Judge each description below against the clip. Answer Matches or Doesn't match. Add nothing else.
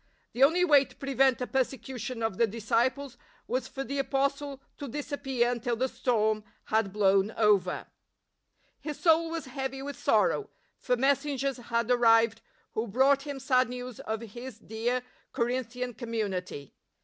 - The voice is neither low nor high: Doesn't match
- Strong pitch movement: Doesn't match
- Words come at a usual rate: Matches